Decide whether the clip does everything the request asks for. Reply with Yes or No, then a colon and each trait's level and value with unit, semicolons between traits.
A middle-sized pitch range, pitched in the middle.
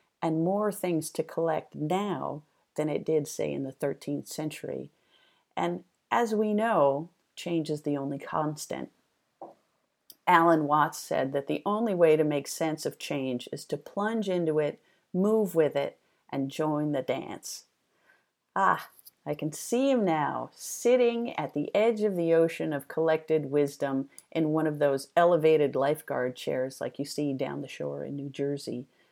Yes: average, 3.5 semitones; medium, 155 Hz